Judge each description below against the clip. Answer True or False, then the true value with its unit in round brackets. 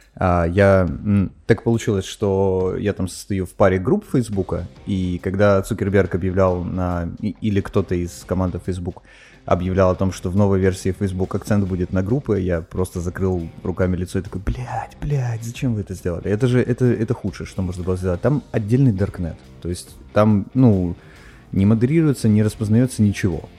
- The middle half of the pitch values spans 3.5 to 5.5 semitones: False (3.0 semitones)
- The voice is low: True (95 Hz)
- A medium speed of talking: False (175 wpm)